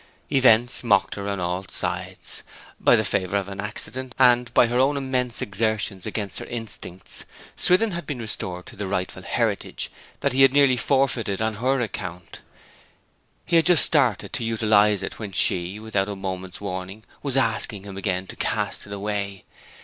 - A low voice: Yes, low, 105 Hz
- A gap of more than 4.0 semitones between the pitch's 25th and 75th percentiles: Yes, average, 4.4 semitones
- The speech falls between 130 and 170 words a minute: No, average, 180 wpm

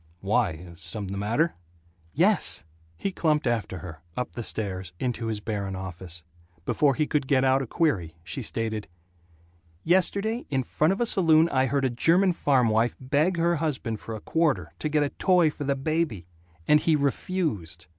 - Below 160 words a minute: No, average, 175 wpm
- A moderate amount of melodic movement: No, wide, 7.3 semitones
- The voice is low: Yes, low, 130 Hz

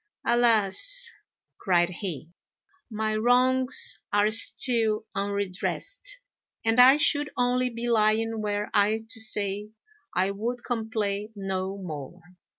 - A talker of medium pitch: No, high, 220 Hz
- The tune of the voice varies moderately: Yes, average, 3.5 semitones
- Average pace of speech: No, slow, 110 wpm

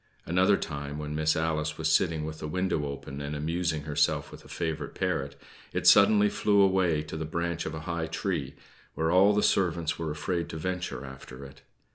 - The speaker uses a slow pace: No, average, 195 wpm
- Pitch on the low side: Yes, very low, 80 Hz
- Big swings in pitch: No, average, 2.9 semitones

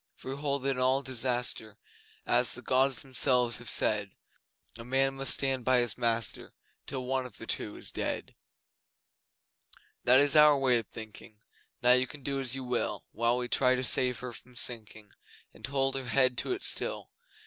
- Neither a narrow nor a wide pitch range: No, narrow, 1.9 semitones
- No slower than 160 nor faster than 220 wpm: Yes, average, 190 wpm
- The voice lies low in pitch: Yes, low, 130 Hz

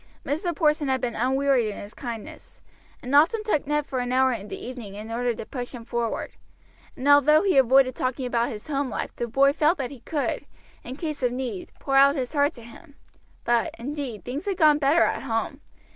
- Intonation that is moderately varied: Yes, average, 3.3 semitones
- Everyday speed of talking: No, fast, 215 wpm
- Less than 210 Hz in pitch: No, very high, 265 Hz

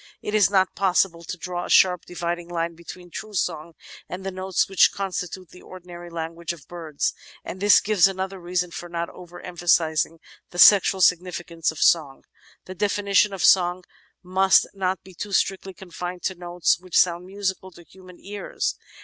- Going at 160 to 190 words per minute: Yes, average, 175 wpm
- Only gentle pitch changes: Yes, narrow, 1.8 semitones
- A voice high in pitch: No, medium, 180 Hz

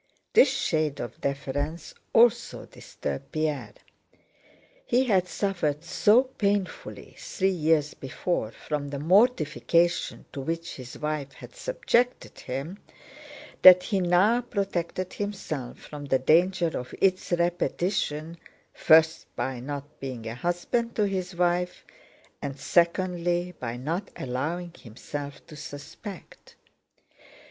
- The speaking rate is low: Yes, slow, 115 wpm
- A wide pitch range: No, average, 4.8 semitones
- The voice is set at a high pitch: No, medium, 170 Hz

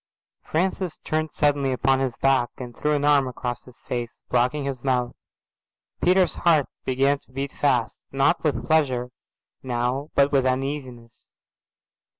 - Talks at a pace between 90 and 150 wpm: Yes, average, 145 wpm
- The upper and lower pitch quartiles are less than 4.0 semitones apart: Yes, average, 2.8 semitones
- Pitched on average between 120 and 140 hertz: Yes, low, 135 Hz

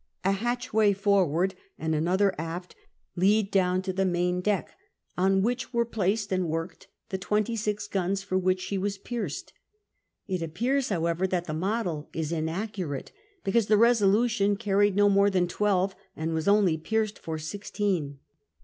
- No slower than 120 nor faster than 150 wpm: No, average, 160 wpm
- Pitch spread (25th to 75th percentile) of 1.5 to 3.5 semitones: Yes, average, 2.8 semitones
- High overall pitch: Yes, high, 195 Hz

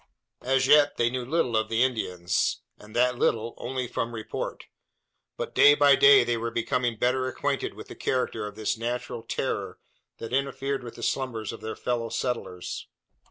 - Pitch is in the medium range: No, low, 120 Hz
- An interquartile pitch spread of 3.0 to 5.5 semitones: No, narrow, 2.5 semitones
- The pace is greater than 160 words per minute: Yes, average, 175 wpm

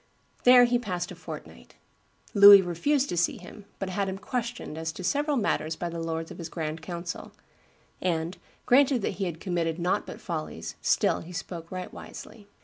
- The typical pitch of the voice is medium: Yes, medium, 180 Hz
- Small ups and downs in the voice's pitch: No, average, 3.9 semitones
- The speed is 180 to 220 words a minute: Yes, average, 185 wpm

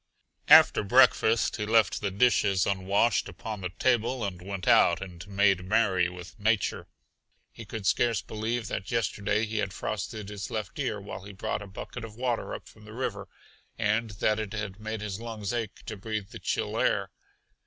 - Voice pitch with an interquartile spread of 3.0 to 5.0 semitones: No, narrow, 2.5 semitones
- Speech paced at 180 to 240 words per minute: Yes, average, 185 wpm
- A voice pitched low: Yes, low, 105 Hz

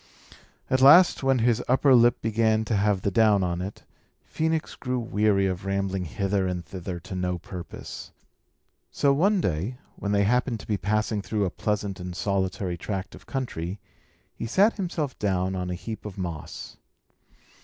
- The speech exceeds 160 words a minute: Yes, average, 170 wpm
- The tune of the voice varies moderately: Yes, average, 4.4 semitones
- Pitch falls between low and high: No, low, 100 Hz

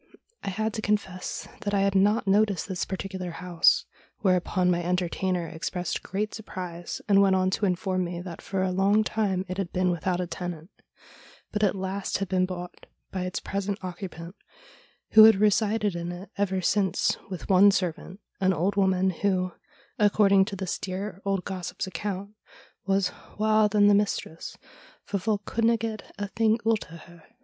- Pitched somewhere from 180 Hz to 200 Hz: Yes, high, 190 Hz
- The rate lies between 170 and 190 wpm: Yes, average, 175 wpm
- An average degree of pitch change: No, narrow, 2.1 semitones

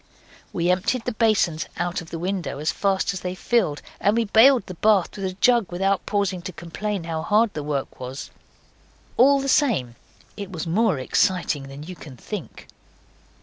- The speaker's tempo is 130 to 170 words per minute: No, average, 185 wpm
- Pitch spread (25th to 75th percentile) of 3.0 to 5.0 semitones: Yes, average, 4.4 semitones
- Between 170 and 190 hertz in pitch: Yes, medium, 185 Hz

